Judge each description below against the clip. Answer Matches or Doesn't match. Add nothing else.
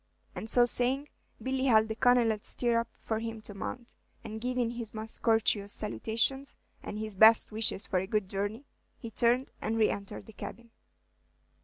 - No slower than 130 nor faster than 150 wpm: Doesn't match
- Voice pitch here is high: Matches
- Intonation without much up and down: Matches